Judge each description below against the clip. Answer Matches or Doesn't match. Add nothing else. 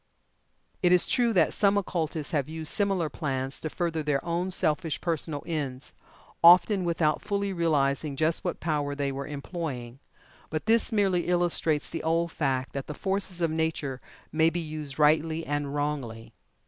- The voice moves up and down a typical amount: Matches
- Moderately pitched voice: Matches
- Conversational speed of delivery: Matches